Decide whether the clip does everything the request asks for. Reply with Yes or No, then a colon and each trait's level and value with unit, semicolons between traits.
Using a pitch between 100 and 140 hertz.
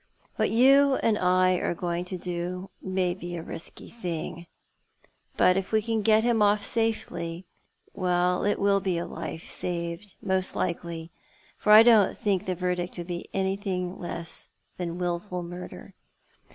No: medium, 180 Hz